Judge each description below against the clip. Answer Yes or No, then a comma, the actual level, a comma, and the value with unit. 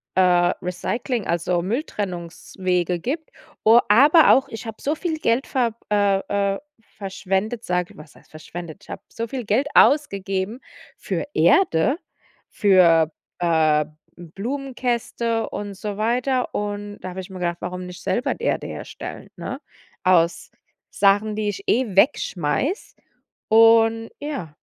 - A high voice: Yes, high, 205 Hz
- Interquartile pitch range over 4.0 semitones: Yes, average, 4.8 semitones